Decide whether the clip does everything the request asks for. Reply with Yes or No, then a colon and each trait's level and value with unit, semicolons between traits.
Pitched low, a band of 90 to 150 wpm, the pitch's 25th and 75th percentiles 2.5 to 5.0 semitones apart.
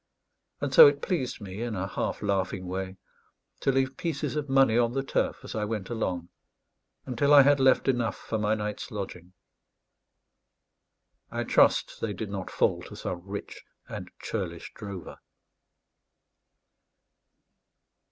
No: low, 110 Hz; average, 140 wpm; wide, 5.5 semitones